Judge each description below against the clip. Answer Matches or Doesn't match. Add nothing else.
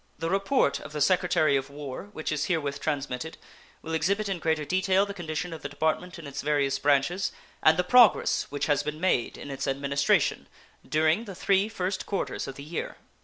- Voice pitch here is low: Doesn't match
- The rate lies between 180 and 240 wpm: Matches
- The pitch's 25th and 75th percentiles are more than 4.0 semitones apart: Matches